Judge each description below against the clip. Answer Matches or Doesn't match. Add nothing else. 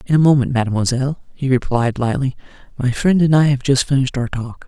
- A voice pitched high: Doesn't match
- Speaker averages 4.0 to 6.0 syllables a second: Doesn't match